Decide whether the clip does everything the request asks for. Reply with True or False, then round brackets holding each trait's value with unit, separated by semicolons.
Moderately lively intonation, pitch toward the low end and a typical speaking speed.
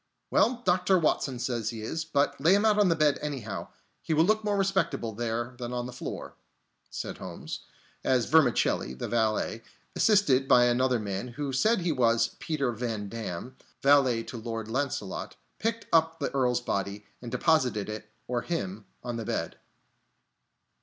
False (5.9 semitones; 125 Hz; 165 wpm)